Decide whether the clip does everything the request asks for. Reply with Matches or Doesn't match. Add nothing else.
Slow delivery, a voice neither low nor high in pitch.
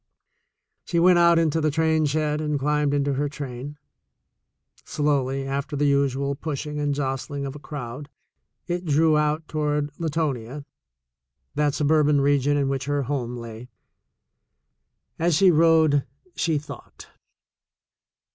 Matches